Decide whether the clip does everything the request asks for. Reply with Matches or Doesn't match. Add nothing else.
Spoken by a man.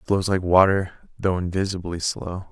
Matches